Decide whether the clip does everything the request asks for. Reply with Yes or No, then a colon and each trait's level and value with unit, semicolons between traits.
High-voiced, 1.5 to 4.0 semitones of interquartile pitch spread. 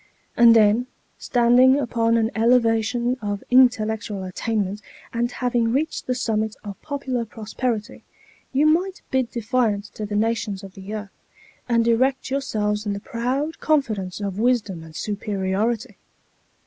Yes: high, 230 Hz; average, 3.2 semitones